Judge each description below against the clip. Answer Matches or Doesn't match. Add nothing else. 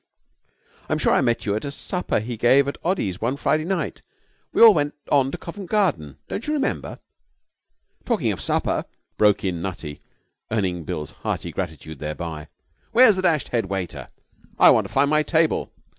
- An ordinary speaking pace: Matches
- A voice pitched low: Matches